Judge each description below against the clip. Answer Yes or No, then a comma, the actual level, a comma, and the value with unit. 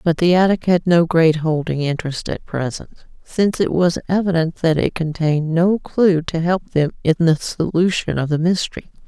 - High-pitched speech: No, medium, 170 Hz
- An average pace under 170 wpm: No, average, 185 wpm